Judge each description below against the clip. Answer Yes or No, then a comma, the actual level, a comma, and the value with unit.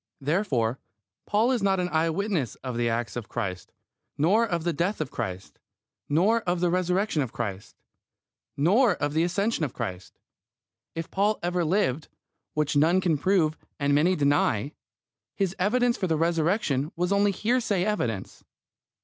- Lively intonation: Yes, wide, 5.7 semitones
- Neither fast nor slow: Yes, average, 160 wpm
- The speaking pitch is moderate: Yes, medium, 170 Hz